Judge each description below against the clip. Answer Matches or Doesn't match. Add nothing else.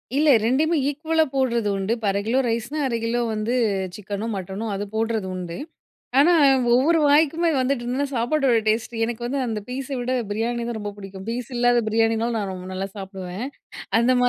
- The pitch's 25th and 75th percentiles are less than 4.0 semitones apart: Matches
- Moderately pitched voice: Doesn't match